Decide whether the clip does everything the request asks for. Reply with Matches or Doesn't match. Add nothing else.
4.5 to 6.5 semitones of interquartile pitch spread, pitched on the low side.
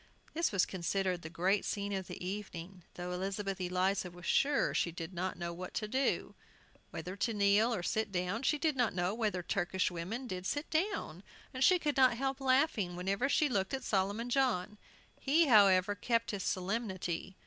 Doesn't match